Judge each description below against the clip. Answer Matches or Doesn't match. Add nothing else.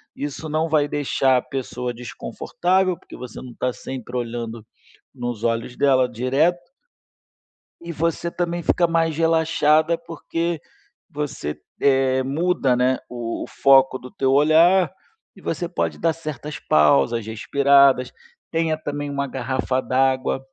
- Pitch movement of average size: Matches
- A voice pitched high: Doesn't match